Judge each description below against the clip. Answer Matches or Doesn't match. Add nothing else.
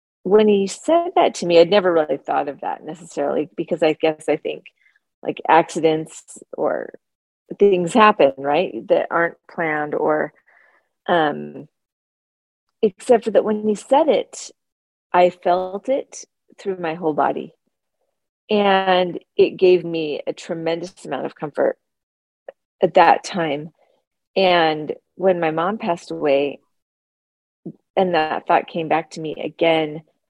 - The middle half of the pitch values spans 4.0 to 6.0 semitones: Matches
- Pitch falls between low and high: Matches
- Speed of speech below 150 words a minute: Matches